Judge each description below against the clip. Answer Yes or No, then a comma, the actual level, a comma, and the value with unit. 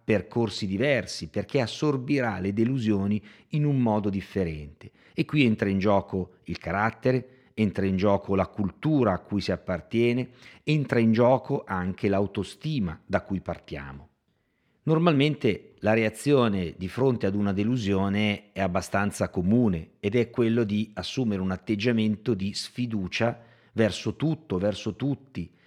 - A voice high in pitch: No, low, 105 Hz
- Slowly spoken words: No, average, 135 wpm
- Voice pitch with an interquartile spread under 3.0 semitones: No, average, 4.0 semitones